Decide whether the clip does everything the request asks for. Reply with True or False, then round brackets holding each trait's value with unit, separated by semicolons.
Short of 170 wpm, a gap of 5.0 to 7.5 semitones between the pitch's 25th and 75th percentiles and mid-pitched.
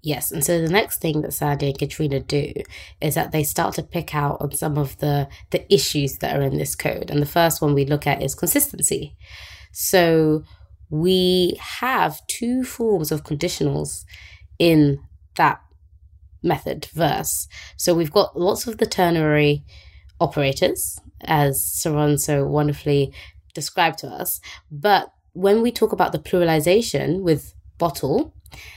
False (150 wpm; 4.1 semitones; 150 Hz)